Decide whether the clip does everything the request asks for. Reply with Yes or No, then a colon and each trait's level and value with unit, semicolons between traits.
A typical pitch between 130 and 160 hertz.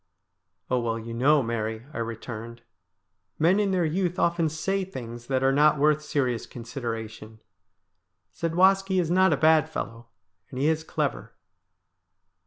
Yes: low, 135 Hz